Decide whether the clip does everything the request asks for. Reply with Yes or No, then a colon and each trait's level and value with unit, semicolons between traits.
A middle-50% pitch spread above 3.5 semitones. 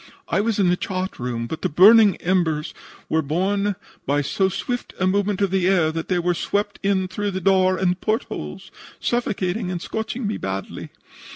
No: average, 3.0 semitones